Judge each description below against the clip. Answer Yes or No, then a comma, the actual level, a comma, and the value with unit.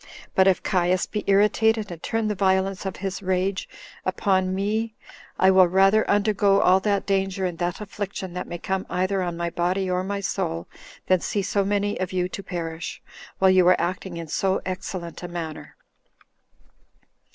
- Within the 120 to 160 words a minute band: No, average, 175 wpm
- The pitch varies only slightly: Yes, narrow, 1.6 semitones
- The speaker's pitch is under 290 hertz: Yes, high, 190 Hz